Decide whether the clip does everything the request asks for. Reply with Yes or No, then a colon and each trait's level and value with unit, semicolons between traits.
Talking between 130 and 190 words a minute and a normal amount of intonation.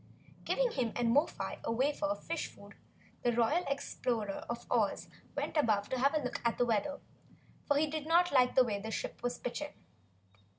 No: average, 200 wpm; average, 4.2 semitones